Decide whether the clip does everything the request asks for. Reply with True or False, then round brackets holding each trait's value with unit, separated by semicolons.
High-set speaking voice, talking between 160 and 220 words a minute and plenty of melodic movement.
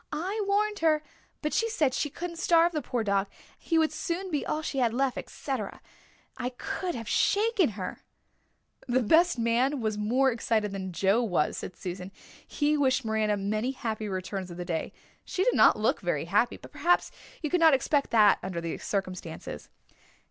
True (250 Hz; 185 wpm; 7.6 semitones)